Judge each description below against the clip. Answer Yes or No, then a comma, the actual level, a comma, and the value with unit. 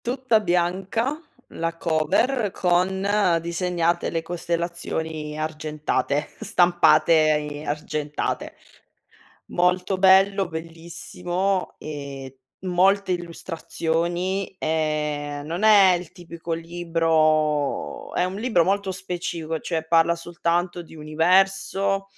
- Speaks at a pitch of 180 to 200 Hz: No, medium, 170 Hz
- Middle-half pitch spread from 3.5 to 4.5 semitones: No, average, 2.8 semitones